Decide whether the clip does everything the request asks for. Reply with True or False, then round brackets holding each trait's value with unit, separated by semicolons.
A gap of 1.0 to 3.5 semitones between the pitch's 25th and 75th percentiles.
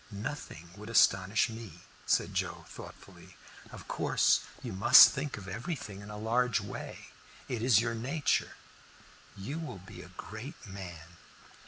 False (4.2 semitones)